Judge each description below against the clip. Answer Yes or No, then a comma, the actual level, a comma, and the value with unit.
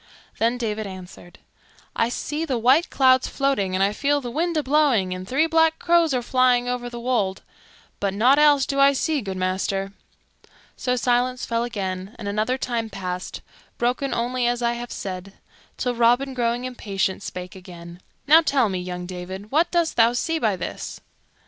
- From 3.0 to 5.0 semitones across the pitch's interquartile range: No, wide, 5.5 semitones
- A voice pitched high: Yes, high, 240 Hz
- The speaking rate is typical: Yes, average, 180 wpm